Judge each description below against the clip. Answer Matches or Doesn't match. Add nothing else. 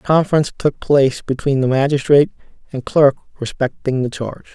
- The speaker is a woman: Doesn't match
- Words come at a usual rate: Matches